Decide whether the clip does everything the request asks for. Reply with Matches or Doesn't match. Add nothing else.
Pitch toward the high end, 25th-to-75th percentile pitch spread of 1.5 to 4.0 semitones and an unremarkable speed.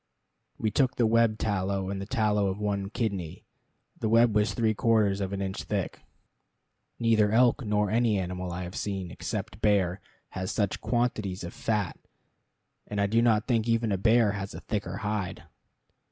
Doesn't match